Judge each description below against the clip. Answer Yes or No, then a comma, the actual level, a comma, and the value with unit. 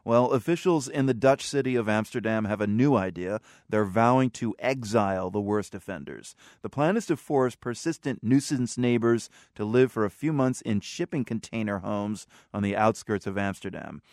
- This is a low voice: Yes, low, 115 Hz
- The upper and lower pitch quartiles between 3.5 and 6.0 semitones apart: Yes, average, 4.2 semitones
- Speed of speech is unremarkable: Yes, average, 180 wpm